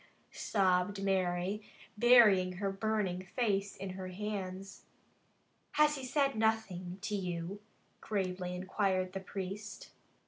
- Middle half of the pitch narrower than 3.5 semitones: Yes, narrow, 2.4 semitones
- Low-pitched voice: No, high, 195 Hz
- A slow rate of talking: Yes, slow, 110 wpm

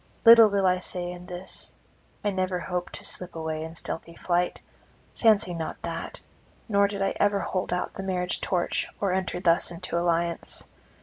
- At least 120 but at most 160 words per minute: No, average, 175 wpm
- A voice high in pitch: No, medium, 180 Hz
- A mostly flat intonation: Yes, narrow, 2.1 semitones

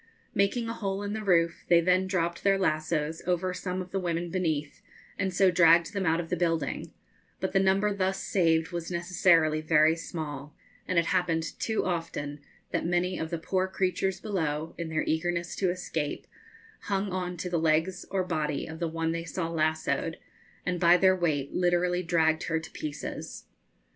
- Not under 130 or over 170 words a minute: No, average, 185 wpm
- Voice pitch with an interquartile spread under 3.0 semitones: Yes, narrow, 2.4 semitones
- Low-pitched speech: No, medium, 170 Hz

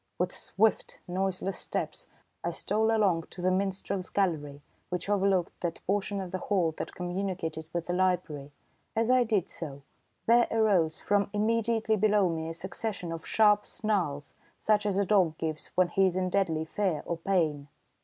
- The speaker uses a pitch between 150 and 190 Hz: Yes, medium, 185 Hz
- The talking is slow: No, average, 170 wpm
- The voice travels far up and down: No, average, 3.6 semitones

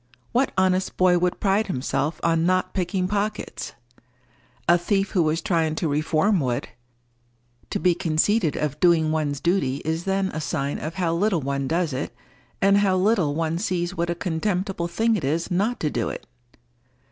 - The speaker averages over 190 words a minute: No, average, 175 wpm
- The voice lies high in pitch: No, medium, 175 Hz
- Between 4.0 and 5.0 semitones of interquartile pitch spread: No, average, 3.5 semitones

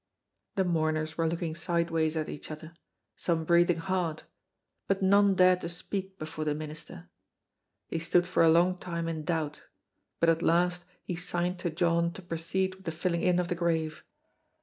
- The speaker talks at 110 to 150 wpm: No, average, 175 wpm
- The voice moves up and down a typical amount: No, narrow, 1.9 semitones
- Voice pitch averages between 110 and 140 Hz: No, medium, 170 Hz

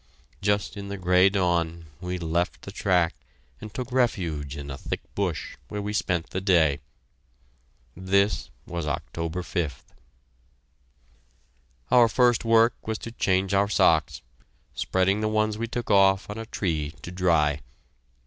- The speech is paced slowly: No, average, 145 wpm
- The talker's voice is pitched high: No, very low, 95 Hz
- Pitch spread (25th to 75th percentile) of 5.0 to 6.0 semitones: No, average, 3.8 semitones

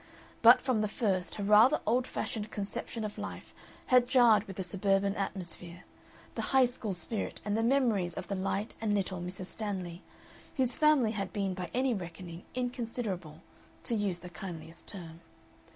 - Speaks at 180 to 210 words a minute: No, average, 170 wpm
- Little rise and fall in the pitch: No, average, 4.3 semitones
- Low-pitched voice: No, high, 205 Hz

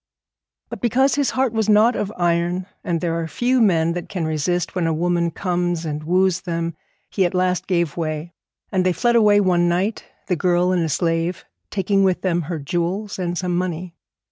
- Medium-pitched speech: Yes, medium, 180 Hz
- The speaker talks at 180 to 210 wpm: Yes, average, 195 wpm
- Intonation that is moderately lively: No, narrow, 2.2 semitones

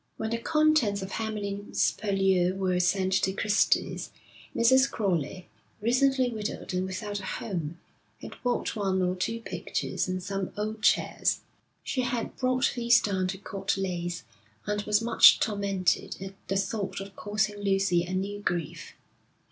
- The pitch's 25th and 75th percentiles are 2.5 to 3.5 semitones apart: Yes, average, 2.8 semitones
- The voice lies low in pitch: No, high, 200 Hz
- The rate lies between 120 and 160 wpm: Yes, average, 150 wpm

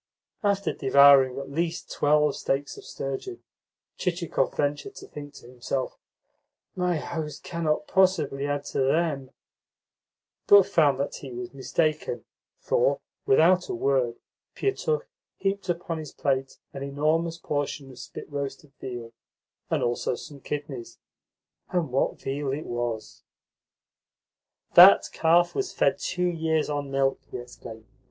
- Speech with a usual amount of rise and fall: Yes, average, 3.7 semitones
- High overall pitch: No, medium, 145 Hz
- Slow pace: Yes, slow, 130 wpm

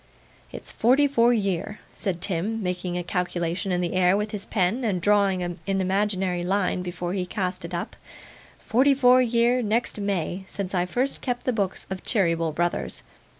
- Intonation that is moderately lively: Yes, average, 3.7 semitones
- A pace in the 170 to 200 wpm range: Yes, average, 175 wpm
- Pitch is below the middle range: No, high, 190 Hz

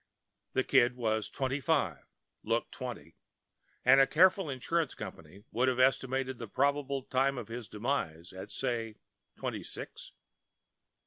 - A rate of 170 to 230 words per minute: No, slow, 135 wpm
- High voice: No, low, 130 Hz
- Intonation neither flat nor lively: Yes, average, 3.2 semitones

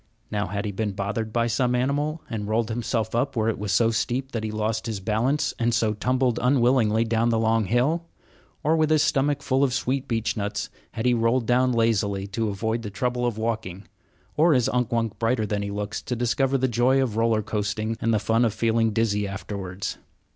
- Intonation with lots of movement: No, average, 2.7 semitones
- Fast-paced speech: Yes, fast, 210 wpm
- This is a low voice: Yes, low, 115 Hz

